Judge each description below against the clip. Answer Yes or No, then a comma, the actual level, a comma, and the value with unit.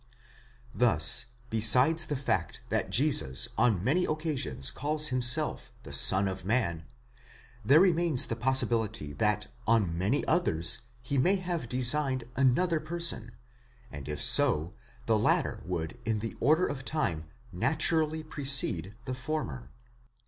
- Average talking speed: No, slow, 130 wpm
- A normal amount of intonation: No, wide, 8.1 semitones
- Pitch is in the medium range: No, low, 125 Hz